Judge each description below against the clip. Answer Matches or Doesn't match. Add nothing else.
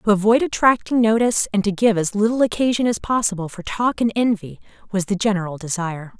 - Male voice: Doesn't match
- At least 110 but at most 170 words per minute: Doesn't match